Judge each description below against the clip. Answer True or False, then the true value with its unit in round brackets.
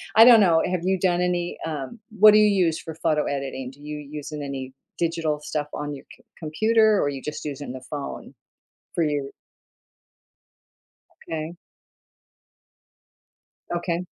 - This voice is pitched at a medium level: True (155 Hz)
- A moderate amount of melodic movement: True (3.4 semitones)